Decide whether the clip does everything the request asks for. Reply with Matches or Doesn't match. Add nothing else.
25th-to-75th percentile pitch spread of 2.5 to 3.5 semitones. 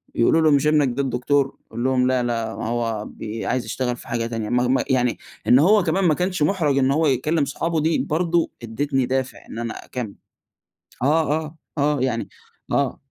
Doesn't match